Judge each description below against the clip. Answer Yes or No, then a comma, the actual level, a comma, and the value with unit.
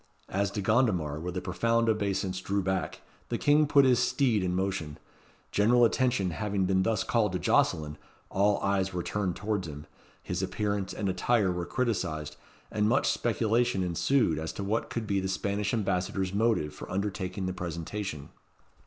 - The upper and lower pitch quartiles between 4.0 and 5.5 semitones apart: No, average, 3.1 semitones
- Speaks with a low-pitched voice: Yes, low, 100 Hz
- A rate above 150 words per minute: Yes, average, 170 wpm